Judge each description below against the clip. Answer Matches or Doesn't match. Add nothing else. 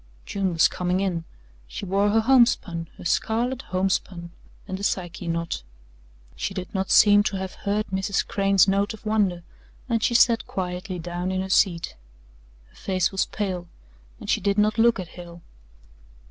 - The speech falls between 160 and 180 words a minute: Matches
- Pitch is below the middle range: Doesn't match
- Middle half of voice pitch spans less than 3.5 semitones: Matches